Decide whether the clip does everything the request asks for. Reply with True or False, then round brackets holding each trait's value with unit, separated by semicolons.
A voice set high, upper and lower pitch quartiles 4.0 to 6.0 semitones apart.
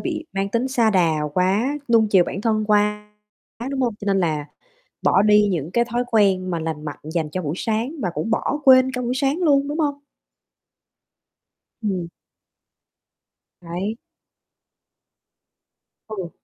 True (210 Hz; 5.4 semitones)